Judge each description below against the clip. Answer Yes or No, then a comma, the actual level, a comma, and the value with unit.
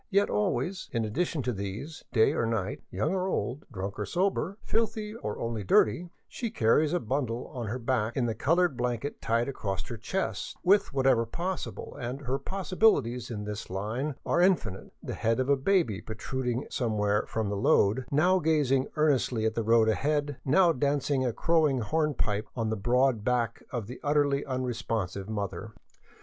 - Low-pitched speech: Yes, low, 125 Hz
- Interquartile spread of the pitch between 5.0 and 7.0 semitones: Yes, wide, 5.5 semitones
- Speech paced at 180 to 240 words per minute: Yes, average, 185 wpm